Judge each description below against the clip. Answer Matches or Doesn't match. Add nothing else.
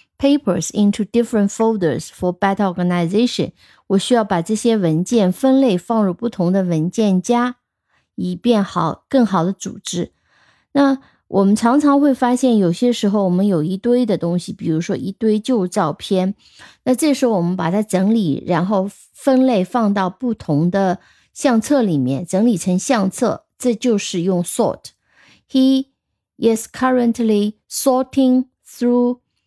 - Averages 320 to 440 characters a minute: Matches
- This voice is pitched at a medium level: Doesn't match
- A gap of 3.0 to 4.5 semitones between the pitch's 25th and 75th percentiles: Doesn't match